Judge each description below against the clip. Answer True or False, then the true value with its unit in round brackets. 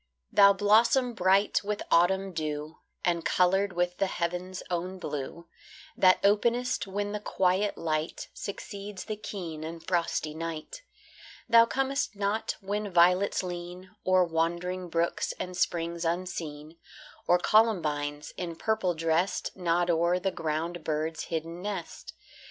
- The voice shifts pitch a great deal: False (3.1 semitones)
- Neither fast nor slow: False (130 wpm)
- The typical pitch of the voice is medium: True (180 Hz)